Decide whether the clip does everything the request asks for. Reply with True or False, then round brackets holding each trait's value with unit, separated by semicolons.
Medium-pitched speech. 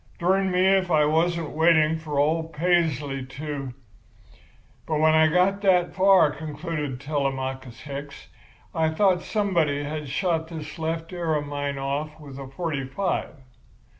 True (155 Hz)